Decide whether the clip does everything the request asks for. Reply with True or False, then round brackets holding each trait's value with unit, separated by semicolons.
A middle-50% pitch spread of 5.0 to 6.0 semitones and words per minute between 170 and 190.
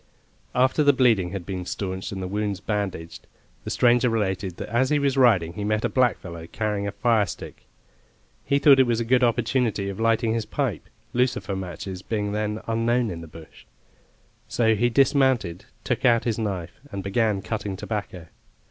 False (4.0 semitones; 180 wpm)